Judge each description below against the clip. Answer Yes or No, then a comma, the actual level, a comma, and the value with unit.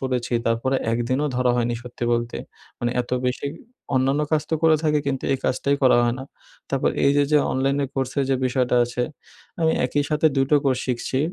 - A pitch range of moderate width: No, narrow, 2.3 semitones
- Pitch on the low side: Yes, low, 130 Hz